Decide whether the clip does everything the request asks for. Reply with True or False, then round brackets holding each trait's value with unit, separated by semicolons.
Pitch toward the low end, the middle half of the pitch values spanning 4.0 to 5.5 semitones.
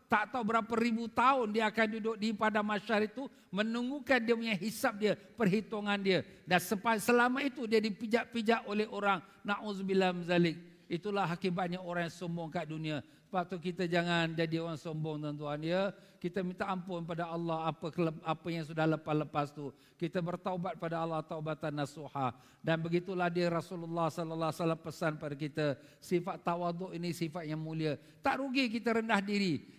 False (180 Hz; 4.7 semitones)